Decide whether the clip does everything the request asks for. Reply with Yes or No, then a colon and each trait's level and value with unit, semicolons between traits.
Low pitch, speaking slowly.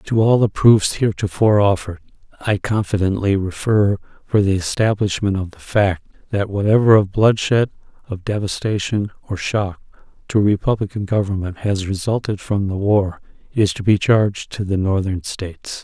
No: low, 100 Hz; average, 150 wpm